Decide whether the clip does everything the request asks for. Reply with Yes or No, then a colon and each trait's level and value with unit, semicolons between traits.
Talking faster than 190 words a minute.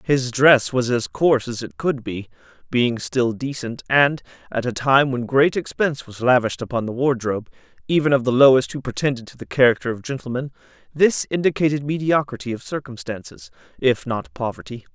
No: average, 175 wpm